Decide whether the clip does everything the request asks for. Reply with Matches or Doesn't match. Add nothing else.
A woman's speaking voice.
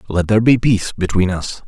Doesn't match